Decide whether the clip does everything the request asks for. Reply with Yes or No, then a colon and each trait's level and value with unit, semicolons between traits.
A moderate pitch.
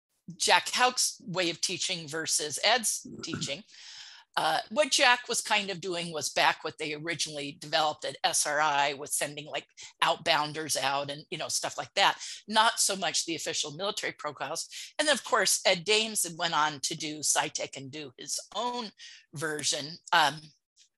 Yes: medium, 165 Hz